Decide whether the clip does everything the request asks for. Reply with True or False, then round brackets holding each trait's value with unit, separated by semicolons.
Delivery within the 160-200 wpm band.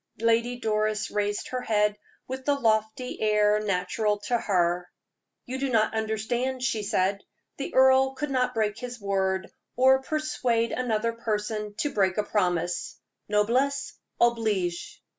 False (140 wpm)